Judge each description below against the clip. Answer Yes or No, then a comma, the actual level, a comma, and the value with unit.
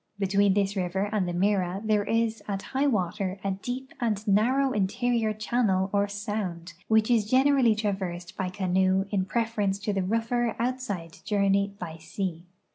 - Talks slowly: No, average, 165 wpm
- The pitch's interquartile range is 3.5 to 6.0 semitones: No, average, 3.0 semitones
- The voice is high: Yes, high, 205 Hz